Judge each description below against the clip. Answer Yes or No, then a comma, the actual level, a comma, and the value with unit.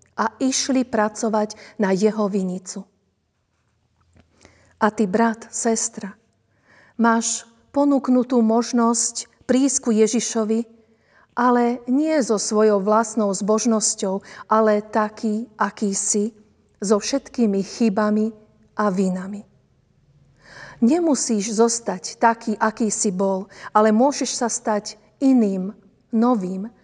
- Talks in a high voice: Yes, high, 220 Hz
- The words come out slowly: Yes, slow, 95 wpm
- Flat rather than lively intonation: Yes, narrow, 2.1 semitones